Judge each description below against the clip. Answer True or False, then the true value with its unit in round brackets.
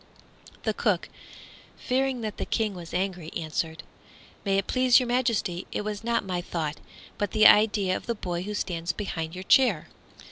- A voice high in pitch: True (195 Hz)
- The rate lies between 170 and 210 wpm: True (175 wpm)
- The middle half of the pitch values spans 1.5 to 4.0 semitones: False (4.4 semitones)